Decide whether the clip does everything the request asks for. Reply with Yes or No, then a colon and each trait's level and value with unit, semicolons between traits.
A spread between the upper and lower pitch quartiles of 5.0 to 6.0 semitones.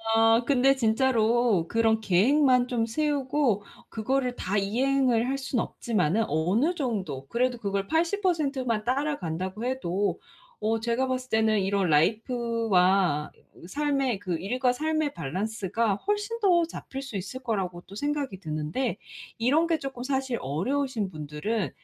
Yes: wide, 5.4 semitones